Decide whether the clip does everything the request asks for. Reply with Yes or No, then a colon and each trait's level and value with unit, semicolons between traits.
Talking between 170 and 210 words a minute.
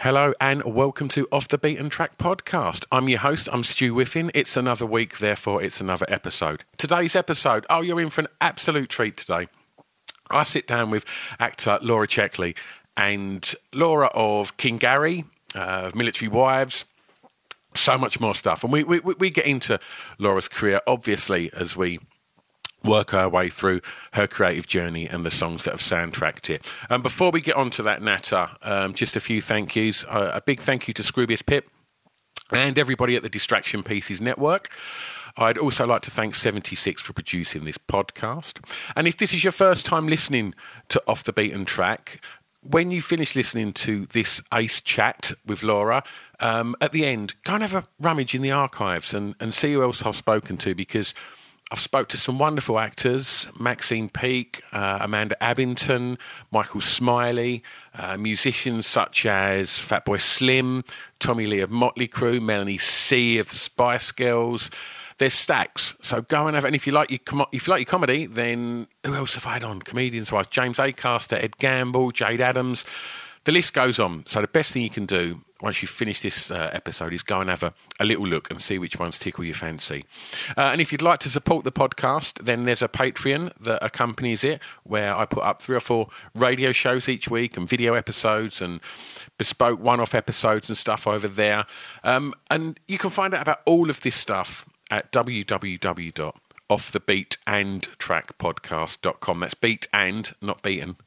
Yes: average, 185 wpm